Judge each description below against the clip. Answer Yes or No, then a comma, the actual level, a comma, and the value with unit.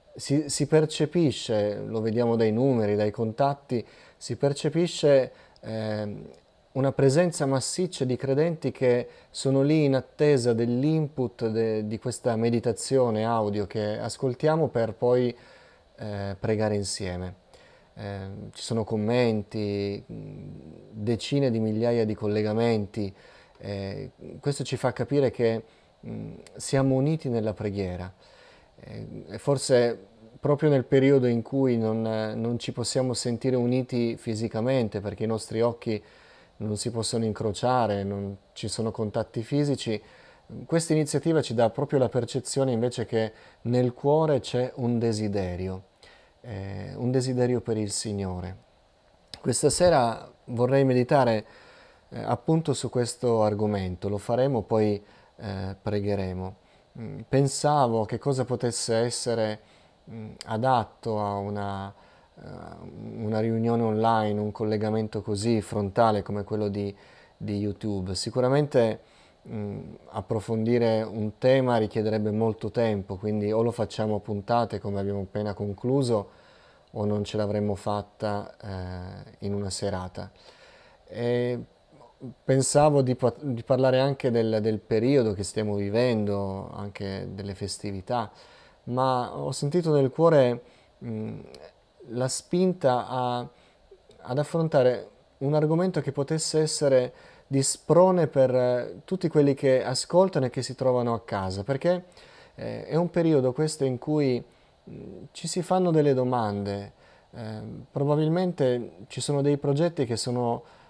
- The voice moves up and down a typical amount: Yes, average, 4.0 semitones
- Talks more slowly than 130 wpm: Yes, average, 120 wpm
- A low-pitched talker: Yes, low, 120 Hz